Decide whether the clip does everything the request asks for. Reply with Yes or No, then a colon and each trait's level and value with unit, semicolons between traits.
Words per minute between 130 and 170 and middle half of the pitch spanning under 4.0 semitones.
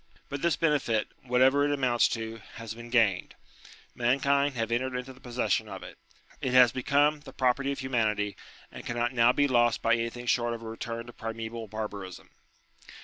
No: average, 180 wpm; narrow, 2.4 semitones